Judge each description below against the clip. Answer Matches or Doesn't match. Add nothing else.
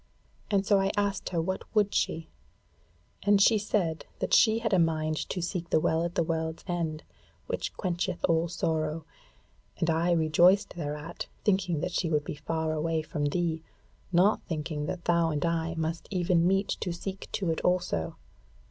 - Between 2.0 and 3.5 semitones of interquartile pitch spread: Matches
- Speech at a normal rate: Matches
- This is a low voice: Doesn't match